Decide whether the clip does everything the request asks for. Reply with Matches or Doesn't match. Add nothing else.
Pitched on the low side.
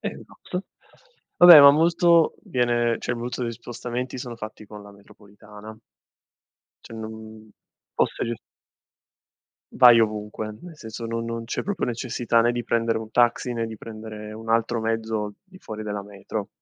Matches